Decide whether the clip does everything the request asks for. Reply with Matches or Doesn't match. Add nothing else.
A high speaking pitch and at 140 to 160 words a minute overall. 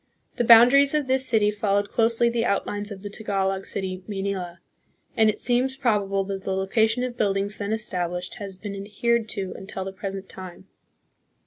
Doesn't match